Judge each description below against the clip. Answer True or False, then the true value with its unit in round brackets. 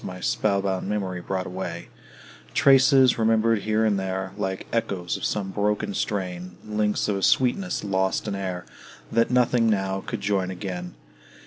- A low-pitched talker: True (100 Hz)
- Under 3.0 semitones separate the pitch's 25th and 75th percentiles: True (2.6 semitones)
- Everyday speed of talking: True (155 wpm)